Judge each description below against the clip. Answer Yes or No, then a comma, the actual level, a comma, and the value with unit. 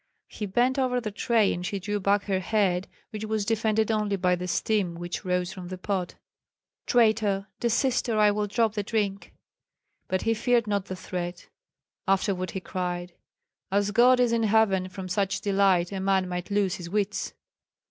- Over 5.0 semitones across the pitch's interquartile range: No, average, 2.8 semitones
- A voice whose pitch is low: No, high, 200 Hz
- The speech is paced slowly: No, average, 180 wpm